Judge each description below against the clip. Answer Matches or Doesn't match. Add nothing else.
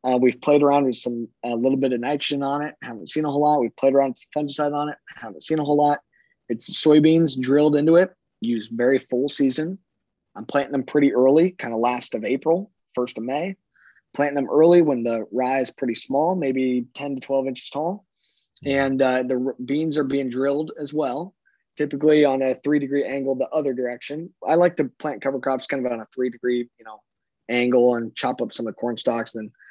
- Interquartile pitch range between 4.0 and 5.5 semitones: Doesn't match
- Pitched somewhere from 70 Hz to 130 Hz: Doesn't match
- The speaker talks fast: Matches